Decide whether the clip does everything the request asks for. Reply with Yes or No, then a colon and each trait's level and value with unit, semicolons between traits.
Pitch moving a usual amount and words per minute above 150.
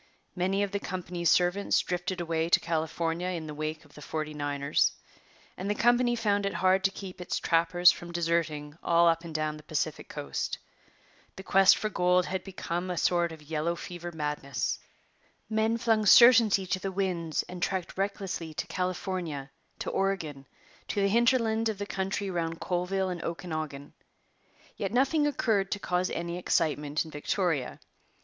Yes: average, 3.3 semitones; average, 170 wpm